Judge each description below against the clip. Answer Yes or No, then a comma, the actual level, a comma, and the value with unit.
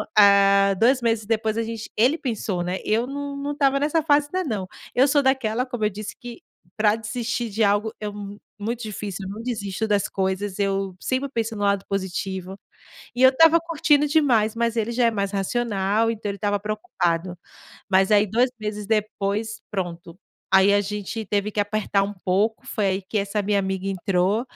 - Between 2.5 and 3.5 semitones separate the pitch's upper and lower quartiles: Yes, average, 3.1 semitones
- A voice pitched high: Yes, high, 210 Hz